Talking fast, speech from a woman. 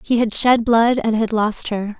Yes: fast, 240 wpm; female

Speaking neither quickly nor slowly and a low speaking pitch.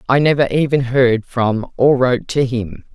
Yes: average, 185 wpm; low, 125 Hz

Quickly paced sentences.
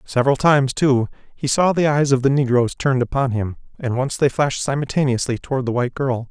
Yes: fast, 210 wpm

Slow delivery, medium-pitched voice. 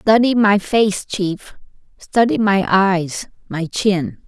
No: slow, 110 wpm; high, 200 Hz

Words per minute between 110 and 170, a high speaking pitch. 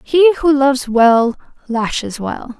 Yes: average, 140 wpm; very high, 265 Hz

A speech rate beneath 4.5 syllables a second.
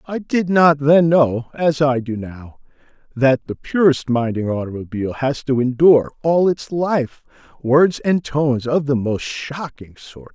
Yes: 4.1 syllables/s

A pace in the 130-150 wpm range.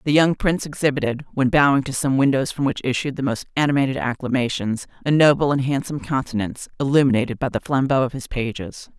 No: average, 185 wpm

